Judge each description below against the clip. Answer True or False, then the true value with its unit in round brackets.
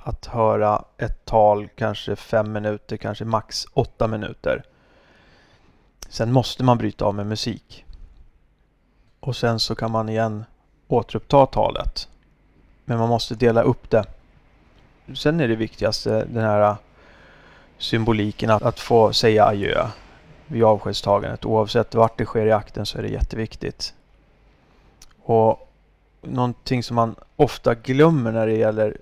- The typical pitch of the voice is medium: False (110 Hz)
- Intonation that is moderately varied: False (2.0 semitones)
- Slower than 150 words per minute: True (135 wpm)